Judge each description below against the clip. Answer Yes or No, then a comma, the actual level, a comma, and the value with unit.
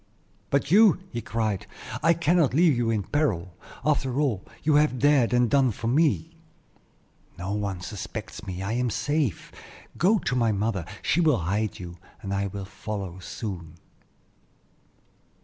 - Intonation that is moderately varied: No, wide, 6.9 semitones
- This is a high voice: No, low, 115 Hz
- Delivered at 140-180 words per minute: Yes, average, 150 wpm